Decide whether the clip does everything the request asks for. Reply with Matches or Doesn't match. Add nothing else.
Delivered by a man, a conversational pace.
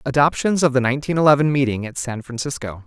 Matches